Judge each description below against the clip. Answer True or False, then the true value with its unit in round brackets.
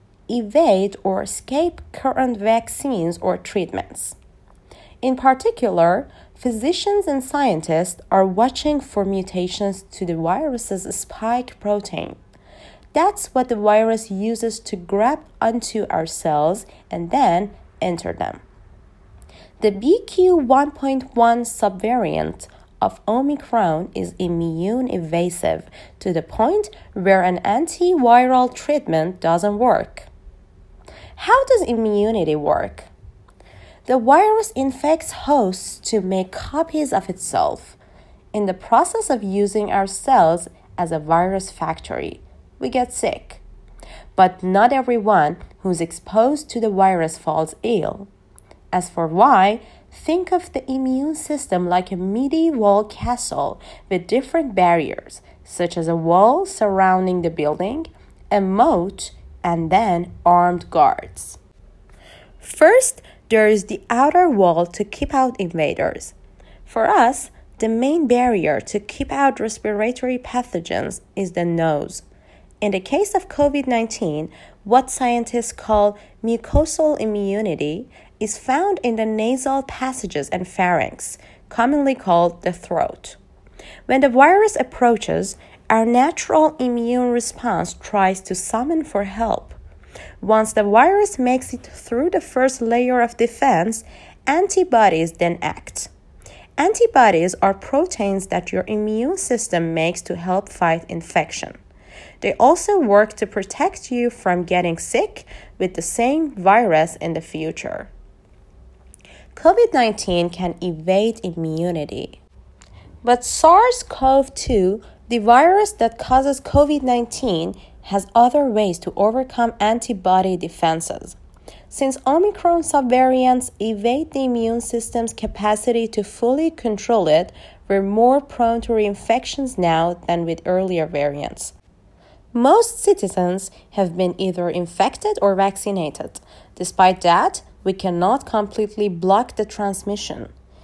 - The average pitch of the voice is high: True (215 Hz)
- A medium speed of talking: True (120 wpm)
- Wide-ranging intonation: True (6.3 semitones)